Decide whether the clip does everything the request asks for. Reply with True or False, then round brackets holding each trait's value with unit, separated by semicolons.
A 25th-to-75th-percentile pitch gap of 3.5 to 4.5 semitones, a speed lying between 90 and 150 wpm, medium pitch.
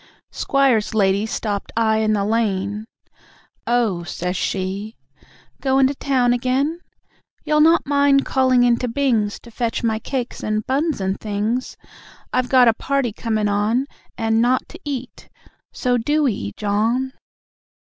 False (3.8 semitones; 140 wpm; 235 Hz)